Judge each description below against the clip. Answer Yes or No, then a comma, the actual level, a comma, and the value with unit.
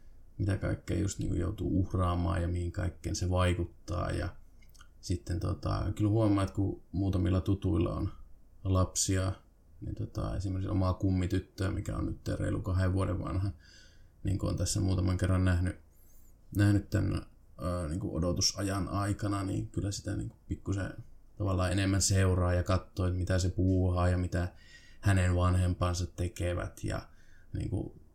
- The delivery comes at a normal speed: Yes, average, 145 wpm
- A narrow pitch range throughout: Yes, narrow, 2.1 semitones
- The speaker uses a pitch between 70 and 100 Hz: Yes, very low, 95 Hz